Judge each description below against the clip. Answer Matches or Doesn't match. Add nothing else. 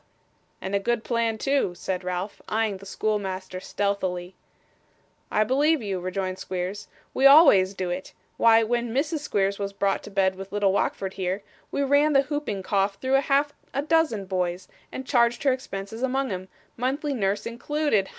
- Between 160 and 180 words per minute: Matches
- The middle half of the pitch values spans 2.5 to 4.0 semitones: Doesn't match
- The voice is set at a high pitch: Matches